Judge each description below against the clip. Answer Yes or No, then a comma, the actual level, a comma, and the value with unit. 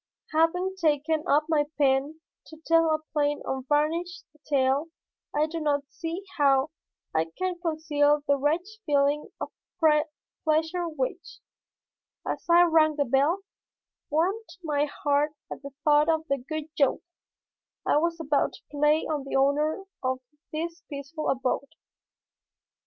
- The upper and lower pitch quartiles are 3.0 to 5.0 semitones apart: No, narrow, 2.4 semitones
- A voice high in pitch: Yes, very high, 305 Hz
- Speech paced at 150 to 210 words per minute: No, slow, 135 wpm